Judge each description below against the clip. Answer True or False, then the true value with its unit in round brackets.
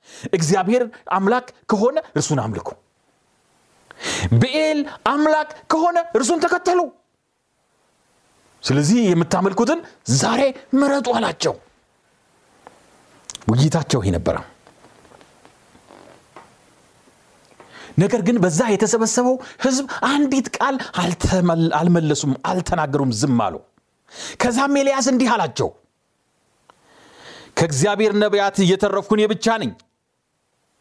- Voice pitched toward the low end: False (220 Hz)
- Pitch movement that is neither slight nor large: False (7.5 semitones)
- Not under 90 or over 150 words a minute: False (75 wpm)